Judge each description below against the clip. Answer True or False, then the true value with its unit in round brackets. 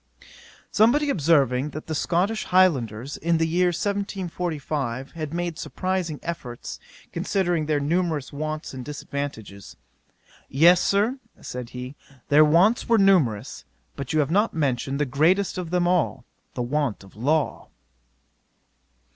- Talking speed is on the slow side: True (130 wpm)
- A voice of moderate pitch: True (155 Hz)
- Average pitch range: True (4.7 semitones)